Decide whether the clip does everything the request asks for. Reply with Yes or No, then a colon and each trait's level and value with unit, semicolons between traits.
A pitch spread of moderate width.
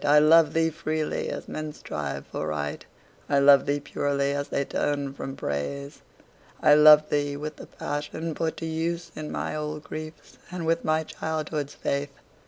No: narrow, 1.8 semitones